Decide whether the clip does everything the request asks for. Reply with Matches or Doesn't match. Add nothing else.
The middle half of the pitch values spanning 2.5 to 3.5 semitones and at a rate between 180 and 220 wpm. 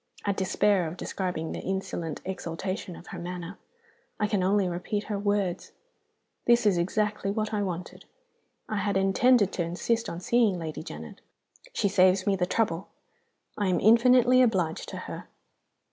Doesn't match